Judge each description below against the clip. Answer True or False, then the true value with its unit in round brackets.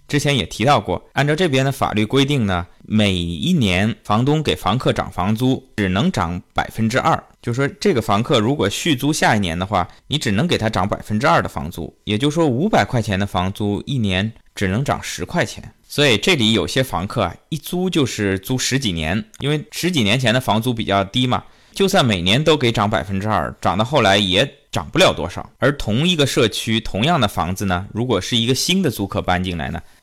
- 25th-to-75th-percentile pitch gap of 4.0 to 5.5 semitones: True (5.2 semitones)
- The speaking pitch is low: True (110 Hz)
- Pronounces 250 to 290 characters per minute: False (315 characters per minute)